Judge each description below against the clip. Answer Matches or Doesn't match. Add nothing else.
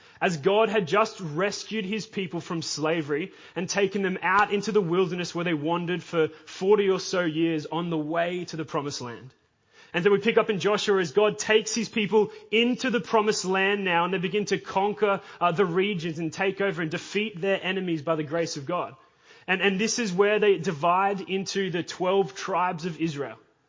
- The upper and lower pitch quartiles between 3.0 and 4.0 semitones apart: Matches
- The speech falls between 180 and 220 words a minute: Matches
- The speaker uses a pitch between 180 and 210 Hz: Matches